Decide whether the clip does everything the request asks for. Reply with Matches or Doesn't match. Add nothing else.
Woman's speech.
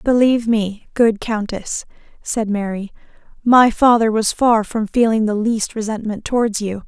Matches